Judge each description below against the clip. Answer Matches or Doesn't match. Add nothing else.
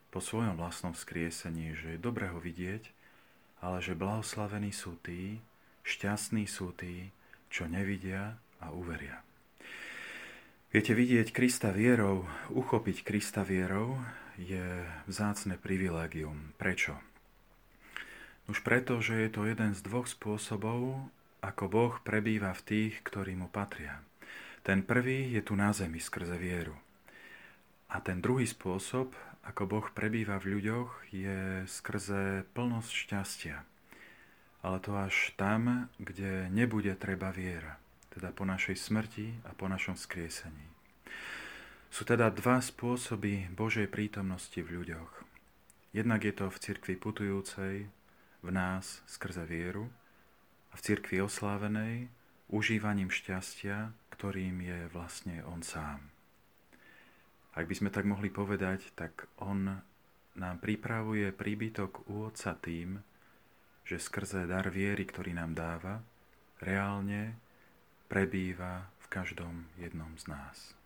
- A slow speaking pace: Doesn't match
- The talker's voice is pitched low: Matches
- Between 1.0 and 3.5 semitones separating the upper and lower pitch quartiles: Matches